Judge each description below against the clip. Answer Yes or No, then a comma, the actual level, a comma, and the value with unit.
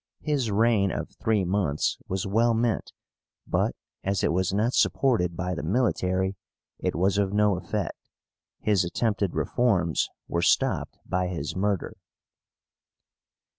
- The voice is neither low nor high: No, low, 100 Hz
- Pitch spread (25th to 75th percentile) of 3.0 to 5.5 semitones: Yes, average, 3.3 semitones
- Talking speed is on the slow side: Yes, slow, 130 wpm